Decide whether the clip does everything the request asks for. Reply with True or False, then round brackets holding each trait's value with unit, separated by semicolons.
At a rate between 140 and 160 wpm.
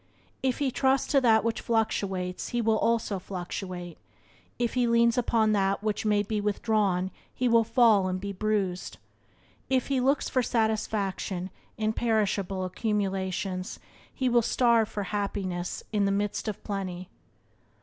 True (150 wpm)